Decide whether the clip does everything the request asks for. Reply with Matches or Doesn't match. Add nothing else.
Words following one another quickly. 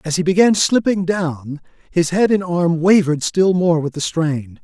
Doesn't match